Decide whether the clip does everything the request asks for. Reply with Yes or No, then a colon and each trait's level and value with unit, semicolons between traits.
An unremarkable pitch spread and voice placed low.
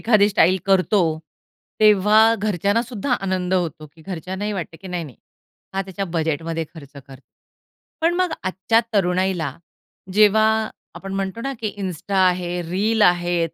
No: average, 3.3 semitones; high, 190 Hz